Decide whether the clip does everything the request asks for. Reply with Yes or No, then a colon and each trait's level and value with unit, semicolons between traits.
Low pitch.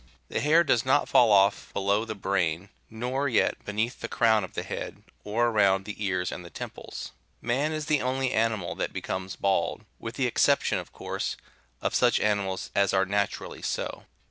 Yes: low, 105 Hz